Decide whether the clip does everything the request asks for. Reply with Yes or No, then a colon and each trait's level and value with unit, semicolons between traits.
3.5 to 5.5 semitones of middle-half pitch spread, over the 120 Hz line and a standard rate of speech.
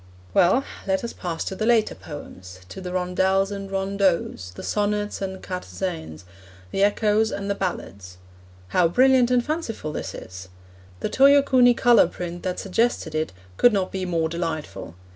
Yes: average, 4.3 semitones; high, 190 Hz; average, 160 wpm